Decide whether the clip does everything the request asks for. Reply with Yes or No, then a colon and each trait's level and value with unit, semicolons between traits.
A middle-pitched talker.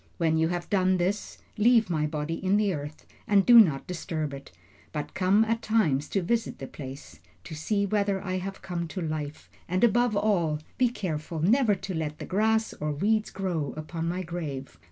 Yes: medium, 180 Hz